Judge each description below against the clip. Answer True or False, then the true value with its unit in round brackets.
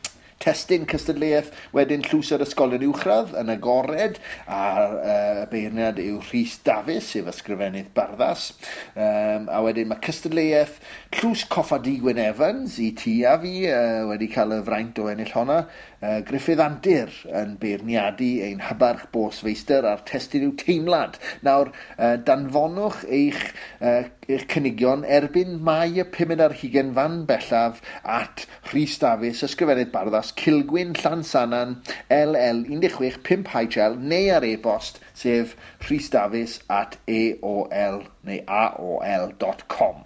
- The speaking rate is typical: False (125 wpm)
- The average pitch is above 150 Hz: False (135 Hz)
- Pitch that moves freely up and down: True (6.3 semitones)